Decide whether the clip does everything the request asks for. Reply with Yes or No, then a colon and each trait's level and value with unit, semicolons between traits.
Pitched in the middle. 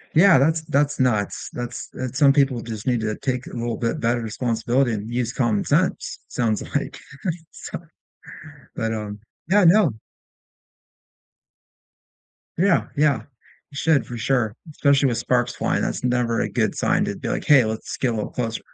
No: low, 125 Hz